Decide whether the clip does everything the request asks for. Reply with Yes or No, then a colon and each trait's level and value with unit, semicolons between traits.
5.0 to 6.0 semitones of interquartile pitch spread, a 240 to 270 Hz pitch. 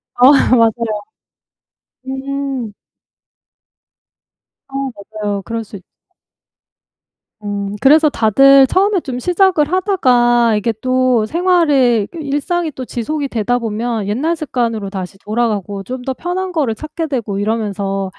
Yes: wide, 5.4 semitones; high, 245 Hz